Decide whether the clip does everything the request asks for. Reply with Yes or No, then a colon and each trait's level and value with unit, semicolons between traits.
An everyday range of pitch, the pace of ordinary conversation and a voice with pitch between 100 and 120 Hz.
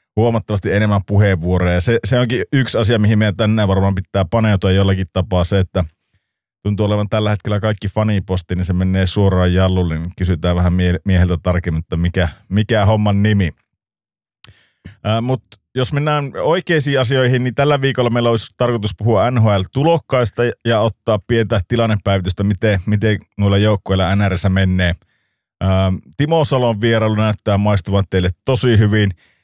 Yes: average, 3.4 semitones; average, 145 wpm; low, 105 Hz